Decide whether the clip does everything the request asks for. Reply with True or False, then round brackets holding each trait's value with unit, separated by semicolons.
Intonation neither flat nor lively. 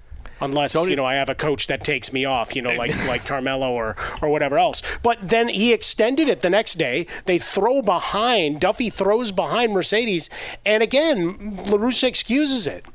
False (8.7 semitones)